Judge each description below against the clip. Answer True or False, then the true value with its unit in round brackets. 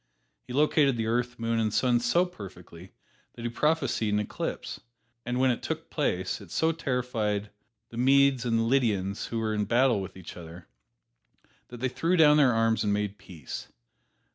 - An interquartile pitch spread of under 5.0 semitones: True (4.0 semitones)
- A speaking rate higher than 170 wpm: True (180 wpm)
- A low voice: True (115 Hz)